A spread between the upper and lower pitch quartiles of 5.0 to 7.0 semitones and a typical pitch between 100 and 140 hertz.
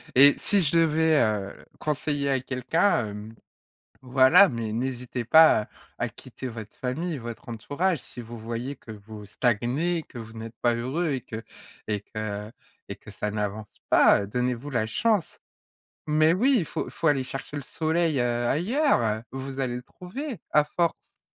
Yes: wide, 5.6 semitones; low, 130 Hz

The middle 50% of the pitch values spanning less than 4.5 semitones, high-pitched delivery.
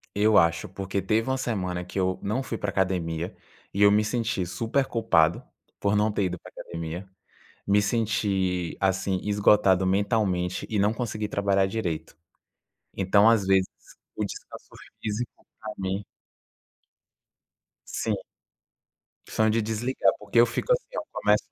No: average, 2.7 semitones; low, 100 Hz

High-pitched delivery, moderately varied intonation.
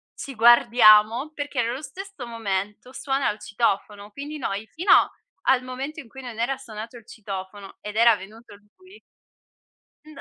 Yes: high, 235 Hz; average, 4.3 semitones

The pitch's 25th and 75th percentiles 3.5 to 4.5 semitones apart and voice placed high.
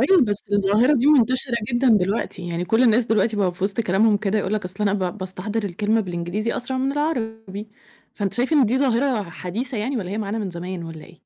Yes: average, 4.0 semitones; high, 215 Hz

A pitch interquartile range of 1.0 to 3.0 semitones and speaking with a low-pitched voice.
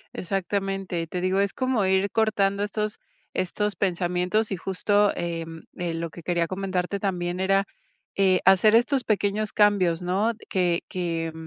No: narrow, 2.5 semitones; high, 190 Hz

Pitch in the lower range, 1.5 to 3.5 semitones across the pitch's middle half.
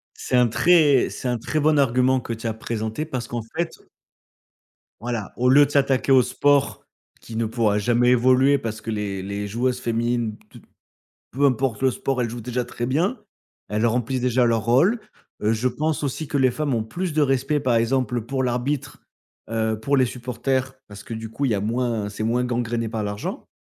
Yes: low, 125 Hz; average, 3.0 semitones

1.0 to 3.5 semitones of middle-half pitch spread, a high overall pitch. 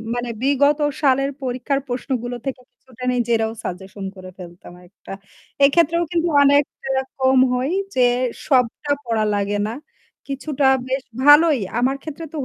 Yes: average, 3.2 semitones; very high, 260 Hz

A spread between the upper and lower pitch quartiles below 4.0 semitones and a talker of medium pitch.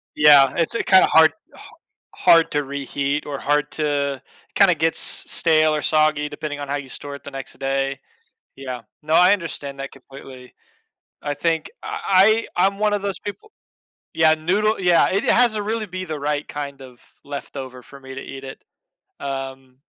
No: average, 4.5 semitones; medium, 150 Hz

